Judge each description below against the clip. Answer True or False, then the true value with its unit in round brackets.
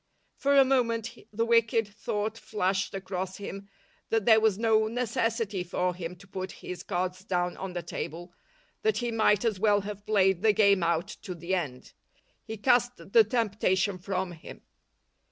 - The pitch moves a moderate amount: True (3.5 semitones)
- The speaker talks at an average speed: True (170 wpm)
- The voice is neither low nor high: False (200 Hz)